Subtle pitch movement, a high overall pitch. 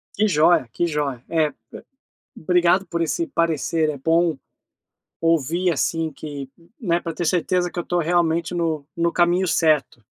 No: narrow, 2.1 semitones; medium, 165 Hz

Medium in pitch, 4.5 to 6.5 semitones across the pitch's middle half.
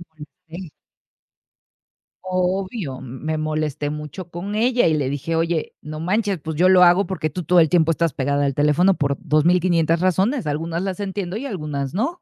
No: medium, 170 Hz; average, 3.5 semitones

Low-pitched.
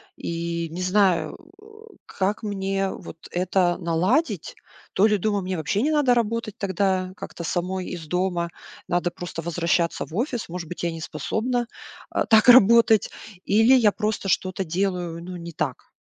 No: high, 190 Hz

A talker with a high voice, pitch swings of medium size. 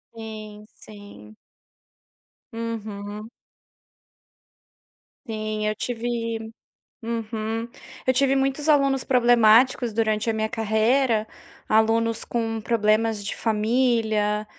No: high, 225 Hz; narrow, 1.7 semitones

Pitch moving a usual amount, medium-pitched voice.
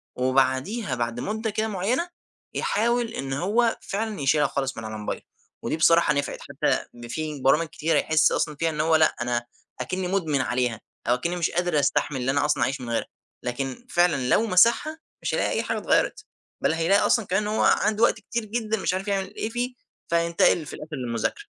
No: wide, 7.7 semitones; medium, 165 Hz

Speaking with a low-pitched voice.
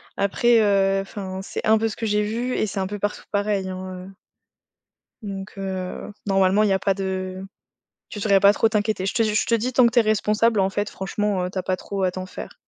No: high, 200 Hz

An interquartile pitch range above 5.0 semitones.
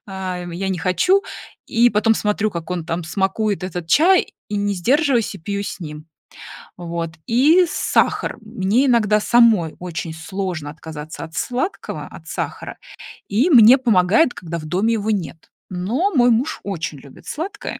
Yes: wide, 5.6 semitones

